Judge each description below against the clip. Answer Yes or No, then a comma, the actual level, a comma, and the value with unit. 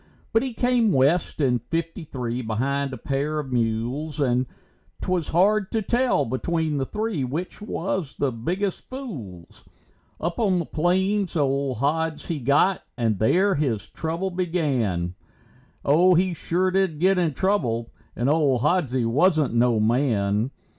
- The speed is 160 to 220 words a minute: No, average, 145 wpm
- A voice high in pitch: No, medium, 150 Hz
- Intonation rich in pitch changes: Yes, wide, 6.6 semitones